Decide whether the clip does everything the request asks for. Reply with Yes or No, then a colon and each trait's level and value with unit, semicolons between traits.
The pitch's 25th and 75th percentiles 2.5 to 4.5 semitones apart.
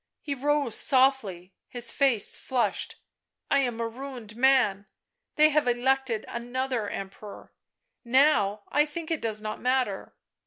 Yes: average, 4.0 semitones